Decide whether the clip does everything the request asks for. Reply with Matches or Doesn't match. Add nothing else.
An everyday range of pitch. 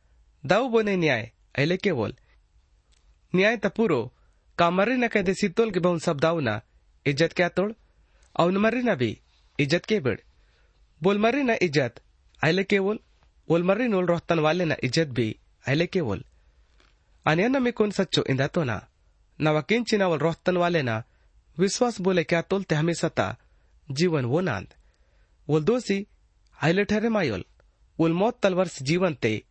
Doesn't match